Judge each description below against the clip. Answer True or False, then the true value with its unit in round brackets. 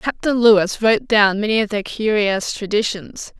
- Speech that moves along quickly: False (160 wpm)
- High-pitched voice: True (210 Hz)